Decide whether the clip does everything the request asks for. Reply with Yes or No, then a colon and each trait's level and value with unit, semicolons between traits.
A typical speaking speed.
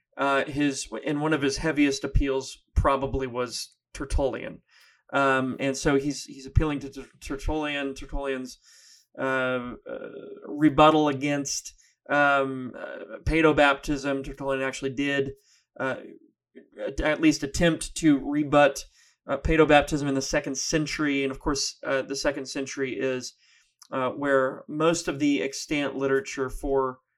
No: slow, 130 wpm